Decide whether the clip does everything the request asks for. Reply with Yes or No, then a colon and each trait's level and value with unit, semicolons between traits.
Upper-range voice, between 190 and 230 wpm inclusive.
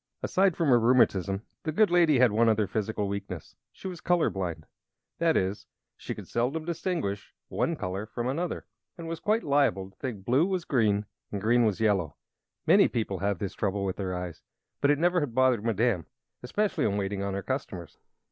No: low, 115 Hz; average, 195 wpm